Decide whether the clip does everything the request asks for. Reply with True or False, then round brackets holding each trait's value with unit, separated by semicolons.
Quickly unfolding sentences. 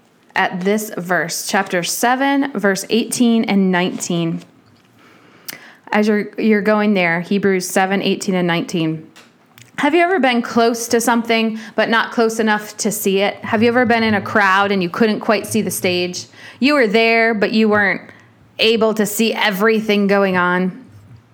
False (165 wpm)